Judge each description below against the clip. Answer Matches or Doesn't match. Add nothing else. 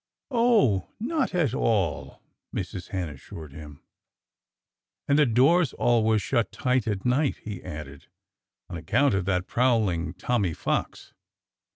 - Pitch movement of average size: Doesn't match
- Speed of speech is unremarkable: Doesn't match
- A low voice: Matches